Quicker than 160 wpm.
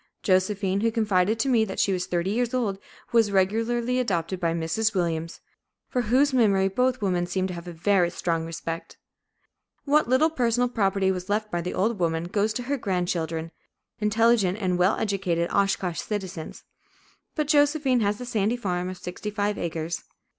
Yes: average, 175 wpm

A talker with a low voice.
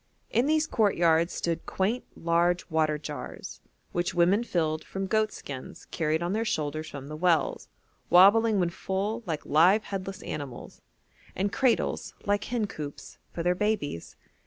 No: medium, 175 Hz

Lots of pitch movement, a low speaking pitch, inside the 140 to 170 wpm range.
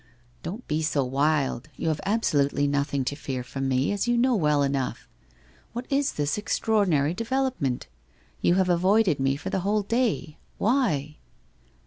No: wide, 7.2 semitones; medium, 155 Hz; average, 165 wpm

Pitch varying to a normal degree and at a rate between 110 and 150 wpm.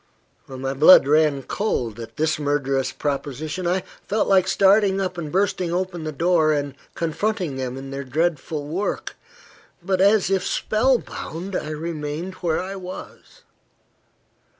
Yes: average, 4.6 semitones; average, 140 wpm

